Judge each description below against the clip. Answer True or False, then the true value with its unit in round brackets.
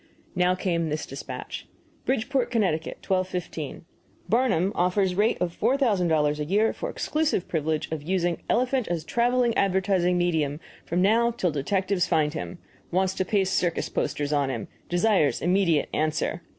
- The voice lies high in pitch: False (180 Hz)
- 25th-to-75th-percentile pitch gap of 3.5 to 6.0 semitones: True (4.6 semitones)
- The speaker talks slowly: False (145 wpm)